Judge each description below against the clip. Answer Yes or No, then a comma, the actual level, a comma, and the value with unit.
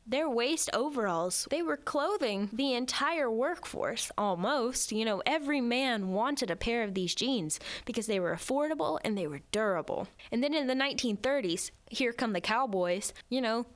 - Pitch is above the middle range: Yes, high, 235 Hz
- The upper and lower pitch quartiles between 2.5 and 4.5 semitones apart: No, average, 4.9 semitones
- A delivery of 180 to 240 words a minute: No, average, 170 wpm